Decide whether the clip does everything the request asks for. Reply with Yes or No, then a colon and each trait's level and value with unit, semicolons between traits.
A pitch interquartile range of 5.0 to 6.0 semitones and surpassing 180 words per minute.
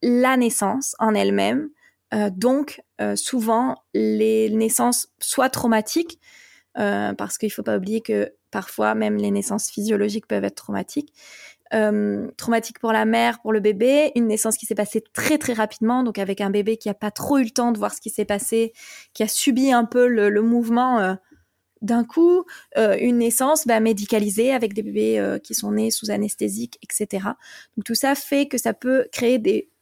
No: average, 3.1 semitones; average, 195 wpm